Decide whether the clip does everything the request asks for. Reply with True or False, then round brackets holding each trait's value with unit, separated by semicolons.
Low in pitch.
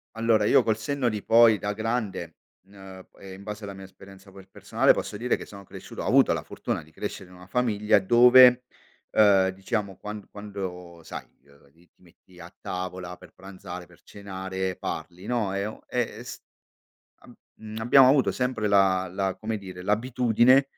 True (100 Hz)